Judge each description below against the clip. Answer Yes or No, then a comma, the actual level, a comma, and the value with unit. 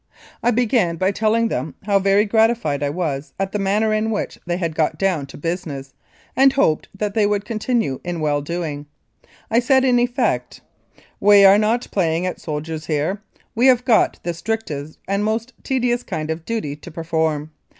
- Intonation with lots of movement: Yes, wide, 5.8 semitones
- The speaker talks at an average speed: Yes, average, 185 wpm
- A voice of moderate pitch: No, high, 195 Hz